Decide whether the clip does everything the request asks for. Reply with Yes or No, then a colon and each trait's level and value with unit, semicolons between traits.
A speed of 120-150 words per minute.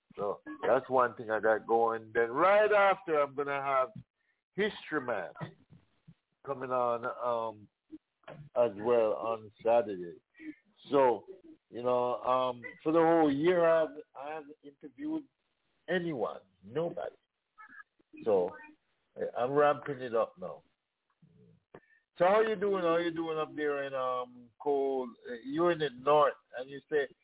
Yes: average, 145 wpm